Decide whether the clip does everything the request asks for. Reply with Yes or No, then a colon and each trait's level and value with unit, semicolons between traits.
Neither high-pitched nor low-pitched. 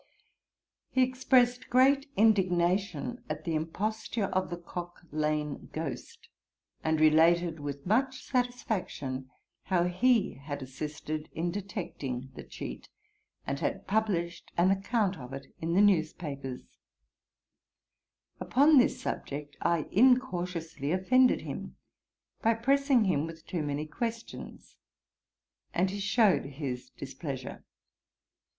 Yes: medium, 175 Hz